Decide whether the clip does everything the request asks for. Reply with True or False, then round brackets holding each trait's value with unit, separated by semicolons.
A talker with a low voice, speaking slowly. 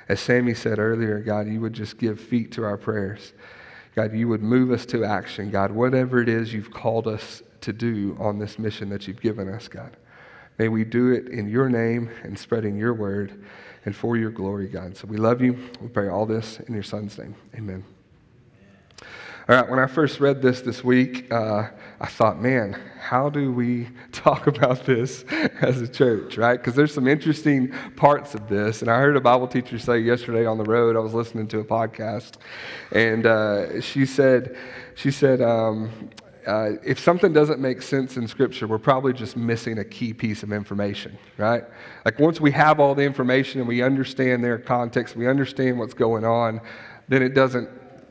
False (115 Hz; 195 wpm)